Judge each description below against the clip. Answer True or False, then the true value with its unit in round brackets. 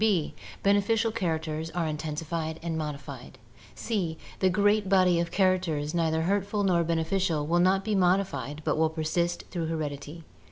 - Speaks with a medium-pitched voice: True (170 Hz)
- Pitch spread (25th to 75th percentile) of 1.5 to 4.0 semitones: True (3.2 semitones)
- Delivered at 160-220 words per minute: False (150 wpm)